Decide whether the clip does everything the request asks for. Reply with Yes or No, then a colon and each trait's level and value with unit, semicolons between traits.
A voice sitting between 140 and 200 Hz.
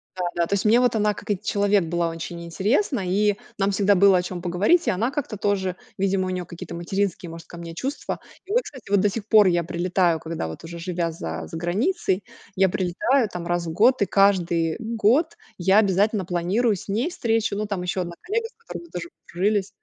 Yes: high, 190 Hz